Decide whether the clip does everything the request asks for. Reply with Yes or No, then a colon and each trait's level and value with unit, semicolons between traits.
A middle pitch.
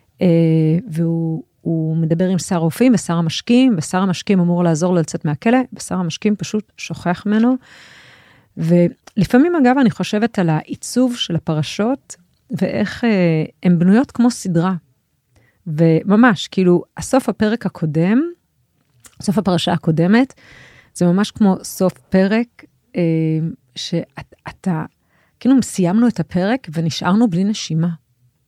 Yes: medium, 180 Hz